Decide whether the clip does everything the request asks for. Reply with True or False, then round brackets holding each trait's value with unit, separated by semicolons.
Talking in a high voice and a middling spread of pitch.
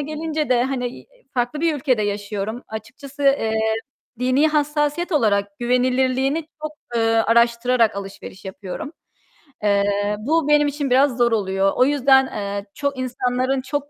True (255 Hz; 4.6 semitones)